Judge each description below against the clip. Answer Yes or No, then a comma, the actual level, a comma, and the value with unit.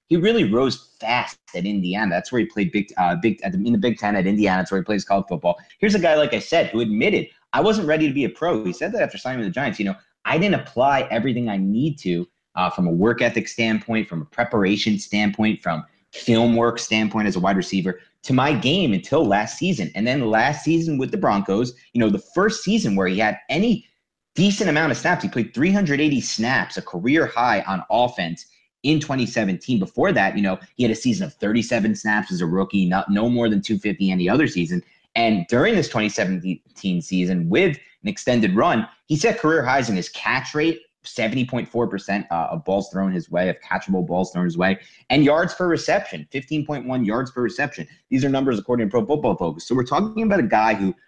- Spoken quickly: Yes, fast, 225 wpm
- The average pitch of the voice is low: Yes, low, 115 Hz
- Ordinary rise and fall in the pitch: No, wide, 7.4 semitones